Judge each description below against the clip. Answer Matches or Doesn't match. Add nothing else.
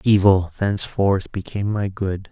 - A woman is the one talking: Doesn't match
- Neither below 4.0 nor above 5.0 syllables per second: Matches